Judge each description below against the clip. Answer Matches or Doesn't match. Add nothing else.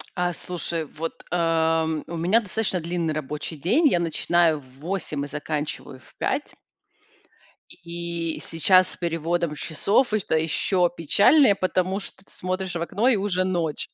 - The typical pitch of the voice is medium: Matches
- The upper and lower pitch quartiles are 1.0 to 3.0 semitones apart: Matches